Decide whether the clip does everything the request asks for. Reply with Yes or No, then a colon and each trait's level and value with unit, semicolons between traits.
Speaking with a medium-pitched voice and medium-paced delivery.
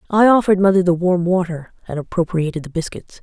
Yes: medium, 180 Hz; average, 185 wpm